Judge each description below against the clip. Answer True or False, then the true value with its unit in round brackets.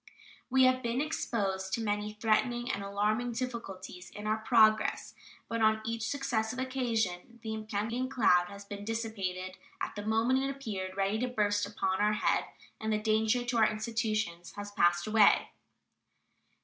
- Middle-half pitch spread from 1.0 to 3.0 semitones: True (2.6 semitones)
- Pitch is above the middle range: True (220 Hz)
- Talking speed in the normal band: True (160 wpm)